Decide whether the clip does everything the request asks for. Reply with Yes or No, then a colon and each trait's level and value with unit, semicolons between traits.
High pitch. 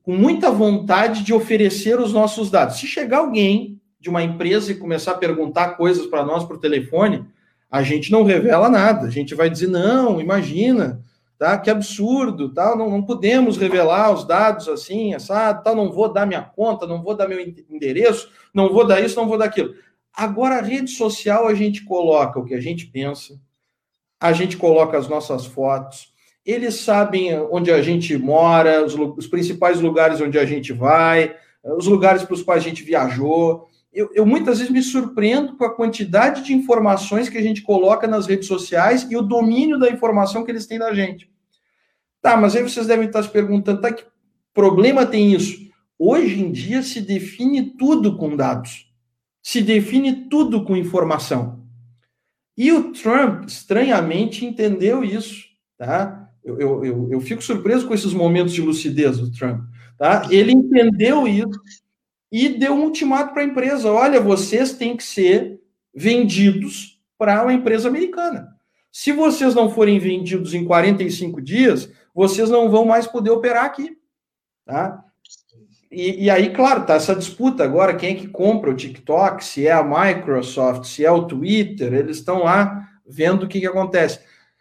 Yes: high, 200 Hz